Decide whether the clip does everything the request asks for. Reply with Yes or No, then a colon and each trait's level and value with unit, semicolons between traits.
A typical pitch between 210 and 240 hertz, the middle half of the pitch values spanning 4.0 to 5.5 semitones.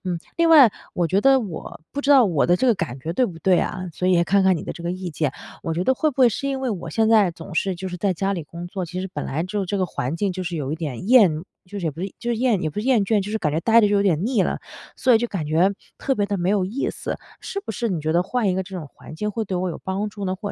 No: high, 190 Hz; average, 4.4 semitones